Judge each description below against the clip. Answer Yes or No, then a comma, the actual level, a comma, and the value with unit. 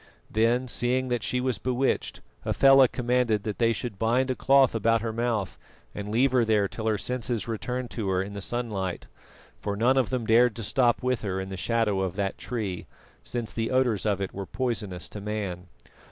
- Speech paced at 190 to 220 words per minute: Yes, average, 200 wpm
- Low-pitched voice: Yes, low, 115 Hz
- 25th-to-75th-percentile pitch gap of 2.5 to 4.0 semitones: Yes, average, 3.4 semitones